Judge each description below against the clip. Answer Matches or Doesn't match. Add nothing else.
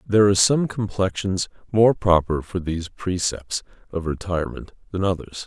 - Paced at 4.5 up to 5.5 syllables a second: Matches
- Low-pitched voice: Matches